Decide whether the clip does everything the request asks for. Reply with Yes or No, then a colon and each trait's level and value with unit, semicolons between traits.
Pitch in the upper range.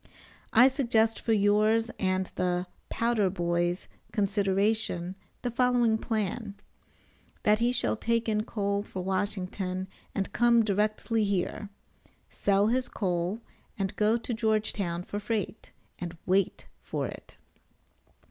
Yes: high, 210 Hz